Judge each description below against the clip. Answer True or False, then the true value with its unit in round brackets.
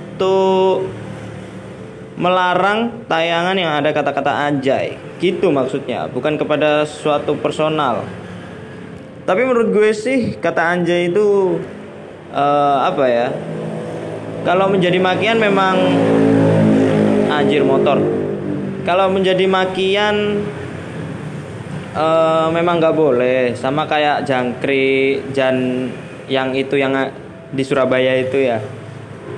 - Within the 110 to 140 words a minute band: False (100 wpm)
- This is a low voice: False (155 Hz)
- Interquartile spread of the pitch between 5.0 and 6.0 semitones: True (5.5 semitones)